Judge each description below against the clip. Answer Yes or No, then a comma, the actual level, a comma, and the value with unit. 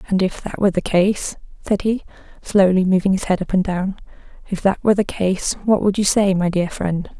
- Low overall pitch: No, high, 190 Hz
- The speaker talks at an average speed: No, fast, 225 wpm